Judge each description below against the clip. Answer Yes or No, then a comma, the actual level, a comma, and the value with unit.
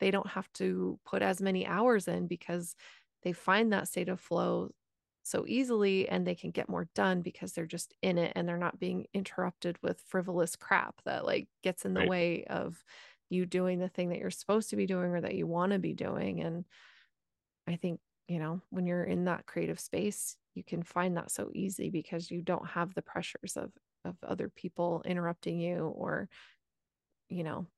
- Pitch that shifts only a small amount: Yes, narrow, 1.7 semitones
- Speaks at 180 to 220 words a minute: Yes, average, 200 wpm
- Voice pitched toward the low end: No, medium, 180 Hz